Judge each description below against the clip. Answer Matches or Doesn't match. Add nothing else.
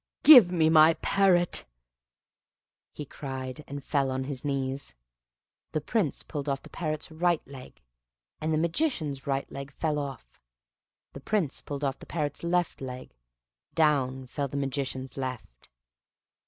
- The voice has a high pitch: Doesn't match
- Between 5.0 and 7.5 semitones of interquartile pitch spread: Doesn't match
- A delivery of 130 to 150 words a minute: Matches